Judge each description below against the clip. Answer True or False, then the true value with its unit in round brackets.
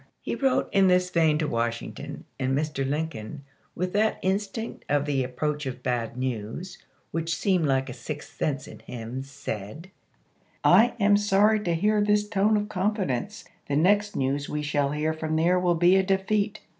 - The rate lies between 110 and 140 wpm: False (185 wpm)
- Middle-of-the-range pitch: True (160 Hz)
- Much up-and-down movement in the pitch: True (6.2 semitones)